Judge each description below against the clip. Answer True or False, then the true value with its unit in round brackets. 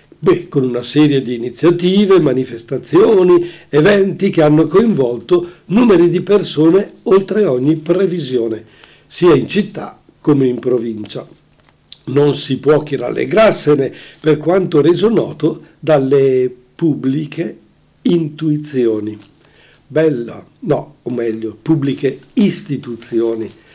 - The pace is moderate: False (105 wpm)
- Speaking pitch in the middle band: True (150 Hz)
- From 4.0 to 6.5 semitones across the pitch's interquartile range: True (5.3 semitones)